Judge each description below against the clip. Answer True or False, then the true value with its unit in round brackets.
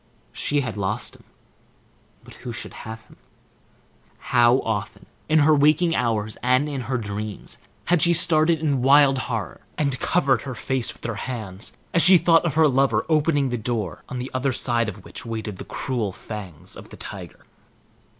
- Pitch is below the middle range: True (125 Hz)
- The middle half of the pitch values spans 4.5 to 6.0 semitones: True (4.8 semitones)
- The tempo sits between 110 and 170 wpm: False (180 wpm)